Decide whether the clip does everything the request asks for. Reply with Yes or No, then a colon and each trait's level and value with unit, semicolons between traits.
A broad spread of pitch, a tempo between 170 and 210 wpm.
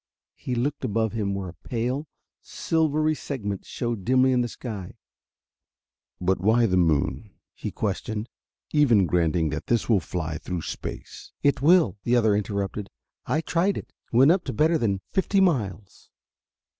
No: wide, 6.3 semitones; average, 155 wpm